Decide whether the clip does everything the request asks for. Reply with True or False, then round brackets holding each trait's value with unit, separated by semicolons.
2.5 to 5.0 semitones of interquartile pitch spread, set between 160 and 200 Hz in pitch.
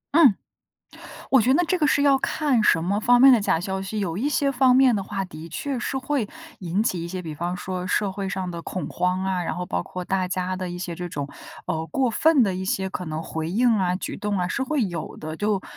False (5.6 semitones; 190 Hz)